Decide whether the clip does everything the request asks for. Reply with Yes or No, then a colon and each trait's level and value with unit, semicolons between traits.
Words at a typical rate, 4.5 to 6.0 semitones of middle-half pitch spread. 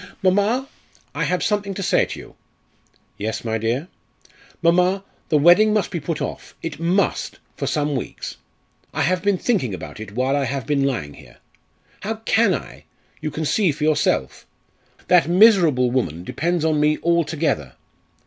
Yes: average, 165 wpm; wide, 5.6 semitones